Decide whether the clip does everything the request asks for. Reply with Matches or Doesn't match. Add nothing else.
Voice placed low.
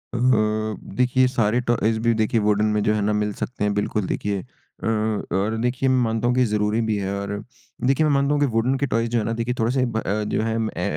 Matches